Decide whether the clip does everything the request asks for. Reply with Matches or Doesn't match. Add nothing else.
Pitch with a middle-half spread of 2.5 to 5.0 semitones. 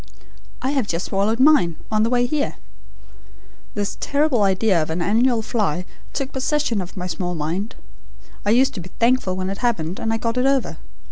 Doesn't match